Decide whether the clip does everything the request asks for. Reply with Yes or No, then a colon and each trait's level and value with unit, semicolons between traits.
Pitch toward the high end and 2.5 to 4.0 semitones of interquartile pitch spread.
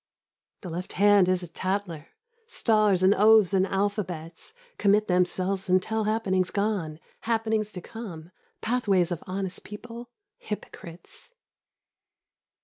Yes: high, 195 Hz; average, 2.9 semitones